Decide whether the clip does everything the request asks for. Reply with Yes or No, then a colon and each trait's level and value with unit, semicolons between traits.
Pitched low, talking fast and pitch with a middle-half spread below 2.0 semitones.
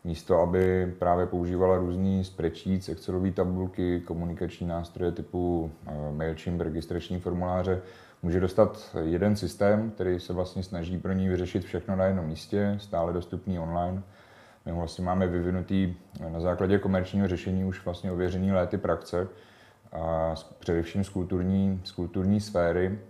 No: very low, 90 Hz; average, 130 wpm; narrow, 1.6 semitones